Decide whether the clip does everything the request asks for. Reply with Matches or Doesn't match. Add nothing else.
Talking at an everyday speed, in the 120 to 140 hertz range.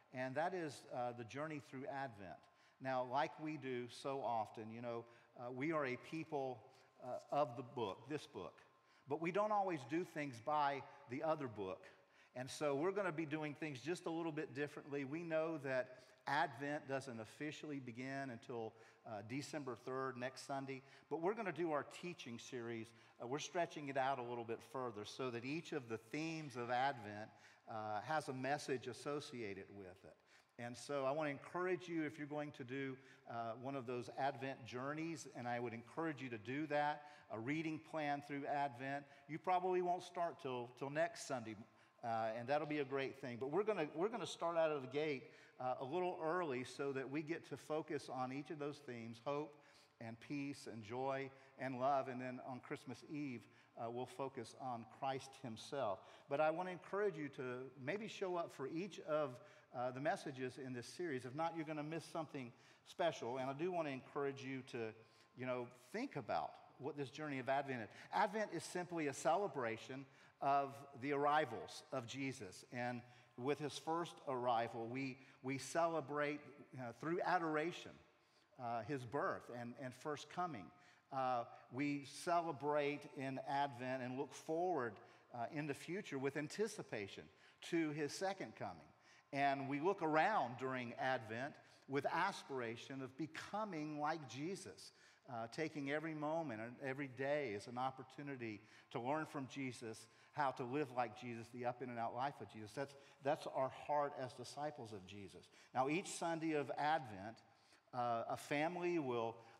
Matches